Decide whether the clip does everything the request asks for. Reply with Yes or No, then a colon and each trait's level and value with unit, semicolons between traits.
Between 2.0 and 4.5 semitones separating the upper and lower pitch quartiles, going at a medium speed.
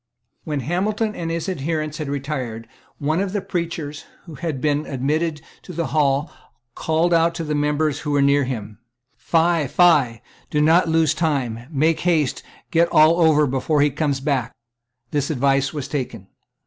Yes: average, 3.0 semitones; average, 170 wpm